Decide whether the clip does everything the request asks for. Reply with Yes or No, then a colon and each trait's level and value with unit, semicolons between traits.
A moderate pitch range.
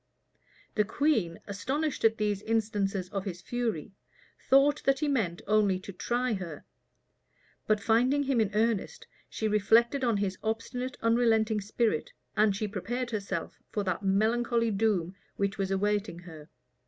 Yes: average, 3.2 semitones